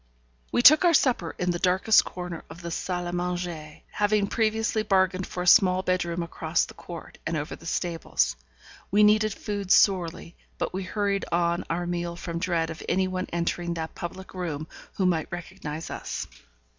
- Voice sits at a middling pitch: Yes, medium, 180 Hz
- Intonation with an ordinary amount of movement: No, narrow, 2.2 semitones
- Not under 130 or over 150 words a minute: No, average, 180 wpm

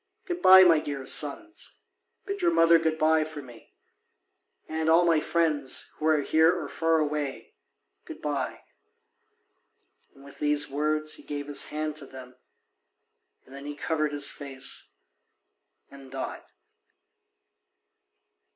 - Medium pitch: Yes, medium, 150 Hz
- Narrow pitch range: Yes, narrow, 2.2 semitones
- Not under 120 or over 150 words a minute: Yes, slow, 135 wpm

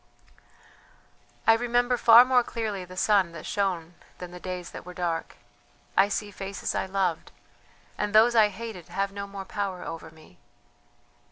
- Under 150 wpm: No, average, 160 wpm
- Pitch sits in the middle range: No, high, 195 Hz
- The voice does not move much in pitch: No, average, 3.4 semitones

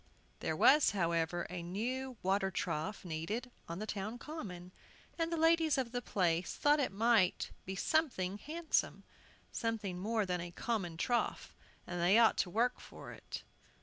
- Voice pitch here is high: Yes, high, 210 Hz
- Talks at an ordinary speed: Yes, average, 165 wpm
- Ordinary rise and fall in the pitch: No, wide, 5.8 semitones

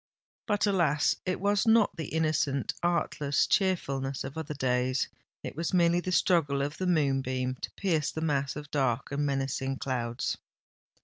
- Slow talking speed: No, average, 145 wpm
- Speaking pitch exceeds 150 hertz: No, medium, 145 Hz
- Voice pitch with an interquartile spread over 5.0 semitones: No, average, 4.3 semitones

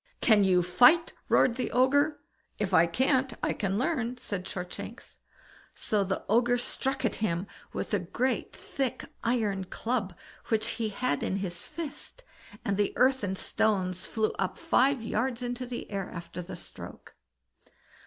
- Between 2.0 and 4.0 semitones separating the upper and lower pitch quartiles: No, average, 4.9 semitones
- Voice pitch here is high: Yes, high, 220 Hz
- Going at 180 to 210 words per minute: No, average, 155 wpm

